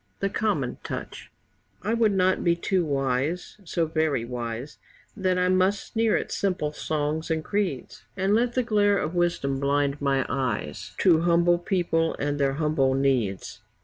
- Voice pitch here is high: No, medium, 165 Hz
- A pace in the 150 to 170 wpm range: Yes, average, 160 wpm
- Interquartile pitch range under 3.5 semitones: No, average, 5.3 semitones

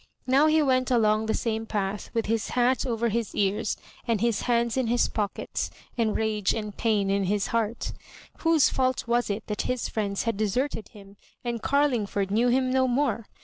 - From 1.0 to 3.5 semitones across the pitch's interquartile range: Yes, average, 3.1 semitones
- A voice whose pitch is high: Yes, high, 230 Hz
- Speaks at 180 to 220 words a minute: Yes, average, 190 wpm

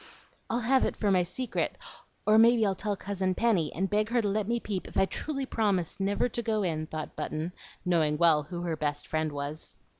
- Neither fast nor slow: No, fast, 215 wpm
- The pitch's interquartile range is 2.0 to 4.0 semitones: No, wide, 5.4 semitones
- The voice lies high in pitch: Yes, high, 195 Hz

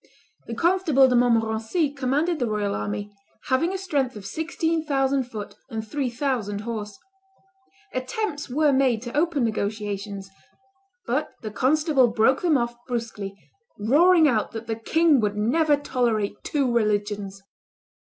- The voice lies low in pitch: No, high, 245 Hz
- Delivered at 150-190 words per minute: No, average, 140 wpm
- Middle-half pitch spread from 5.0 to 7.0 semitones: Yes, average, 5.3 semitones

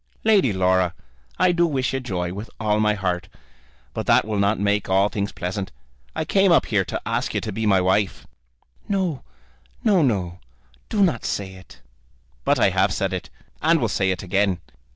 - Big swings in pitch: Yes, wide, 5.9 semitones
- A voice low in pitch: Yes, low, 105 Hz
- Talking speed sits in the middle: Yes, average, 190 wpm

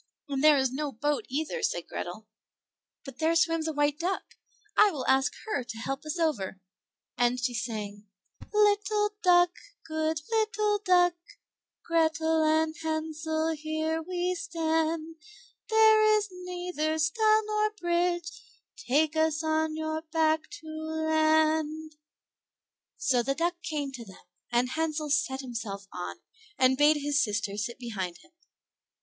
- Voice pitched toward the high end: Yes, very high, 315 Hz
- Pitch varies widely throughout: No, average, 3.5 semitones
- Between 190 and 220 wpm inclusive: No, average, 140 wpm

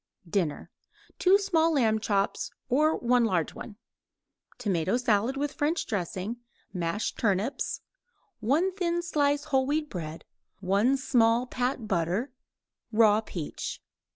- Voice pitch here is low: No, high, 235 Hz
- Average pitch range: No, wide, 6.3 semitones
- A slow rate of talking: Yes, slow, 120 wpm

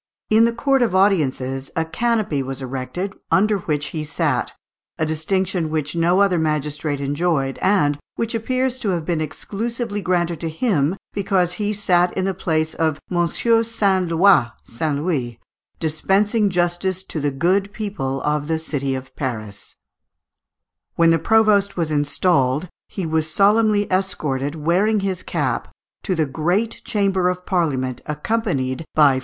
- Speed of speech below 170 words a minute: Yes, average, 155 wpm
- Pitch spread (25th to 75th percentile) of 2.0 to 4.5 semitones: No, average, 5.0 semitones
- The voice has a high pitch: No, medium, 170 Hz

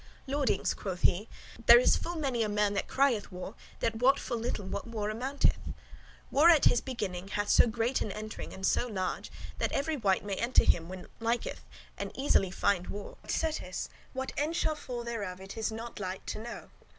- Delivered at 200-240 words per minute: Yes, fast, 205 wpm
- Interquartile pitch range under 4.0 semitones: No, average, 4.6 semitones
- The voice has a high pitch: Yes, high, 225 Hz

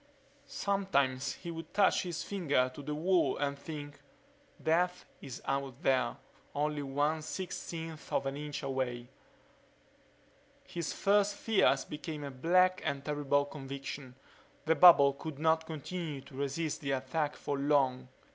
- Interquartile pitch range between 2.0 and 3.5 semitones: Yes, average, 3.2 semitones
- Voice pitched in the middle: Yes, medium, 145 Hz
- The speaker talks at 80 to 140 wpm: Yes, slow, 135 wpm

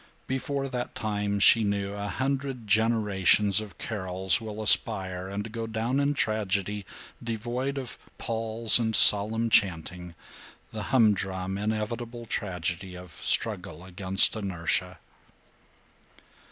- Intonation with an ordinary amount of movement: Yes, average, 3.3 semitones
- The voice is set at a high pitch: No, low, 105 Hz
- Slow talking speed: Yes, slow, 115 wpm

